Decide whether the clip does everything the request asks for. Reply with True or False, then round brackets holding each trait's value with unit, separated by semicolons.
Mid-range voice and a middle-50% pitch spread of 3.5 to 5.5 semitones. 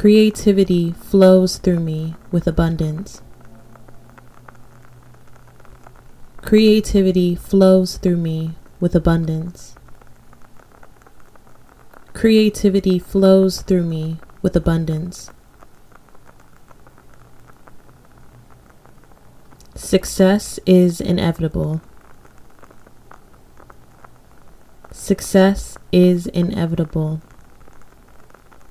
False (175 Hz; 2.9 semitones)